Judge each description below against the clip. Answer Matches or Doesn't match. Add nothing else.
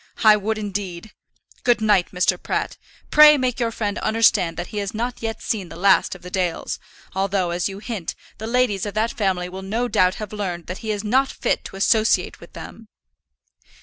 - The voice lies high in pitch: Matches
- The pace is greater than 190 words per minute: Matches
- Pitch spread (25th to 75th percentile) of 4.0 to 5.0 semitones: Doesn't match